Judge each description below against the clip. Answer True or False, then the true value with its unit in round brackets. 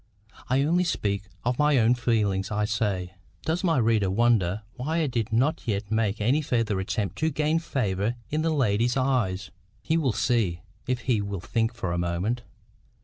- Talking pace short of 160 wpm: False (180 wpm)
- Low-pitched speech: True (115 Hz)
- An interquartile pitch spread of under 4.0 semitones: False (4.9 semitones)